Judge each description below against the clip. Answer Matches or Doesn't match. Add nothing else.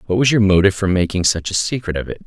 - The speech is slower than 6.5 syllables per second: Doesn't match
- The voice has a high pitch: Doesn't match